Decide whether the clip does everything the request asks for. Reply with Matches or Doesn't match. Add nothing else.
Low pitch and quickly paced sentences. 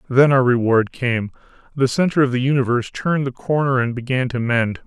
Doesn't match